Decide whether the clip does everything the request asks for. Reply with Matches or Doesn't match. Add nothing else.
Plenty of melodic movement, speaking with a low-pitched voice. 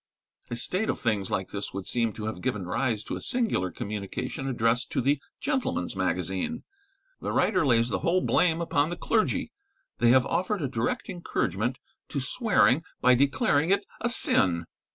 Matches